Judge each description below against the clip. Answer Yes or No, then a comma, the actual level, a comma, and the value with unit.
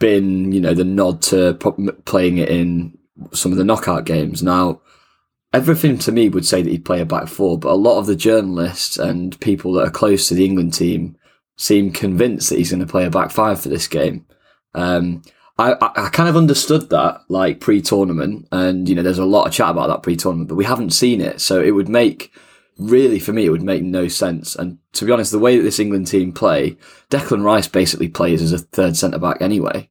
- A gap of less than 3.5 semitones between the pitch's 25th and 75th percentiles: Yes, average, 2.9 semitones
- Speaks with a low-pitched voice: Yes, very low, 90 Hz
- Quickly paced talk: Yes, fast, 225 wpm